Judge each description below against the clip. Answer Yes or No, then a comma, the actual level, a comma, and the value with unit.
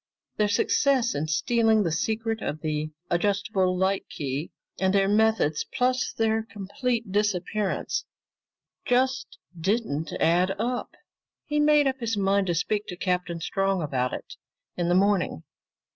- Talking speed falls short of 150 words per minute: Yes, average, 140 wpm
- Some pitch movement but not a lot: Yes, average, 4.4 semitones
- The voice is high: Yes, high, 200 Hz